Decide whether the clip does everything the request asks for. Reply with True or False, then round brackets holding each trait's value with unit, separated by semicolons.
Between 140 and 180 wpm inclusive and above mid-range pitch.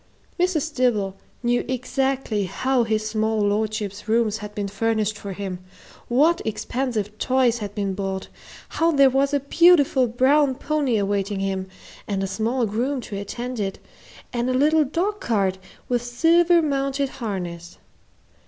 True (145 wpm; 235 Hz)